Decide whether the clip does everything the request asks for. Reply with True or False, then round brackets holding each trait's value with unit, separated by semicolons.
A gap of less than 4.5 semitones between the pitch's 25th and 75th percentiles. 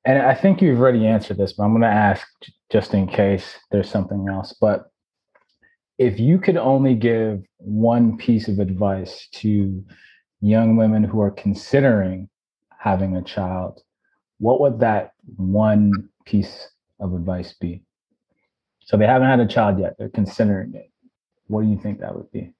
True (3.2 semitones)